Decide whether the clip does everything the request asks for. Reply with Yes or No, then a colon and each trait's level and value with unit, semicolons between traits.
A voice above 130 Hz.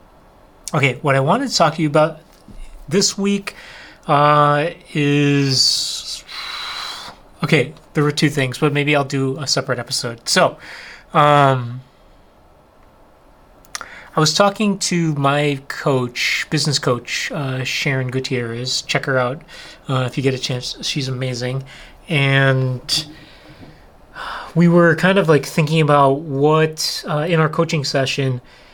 Yes: medium, 140 Hz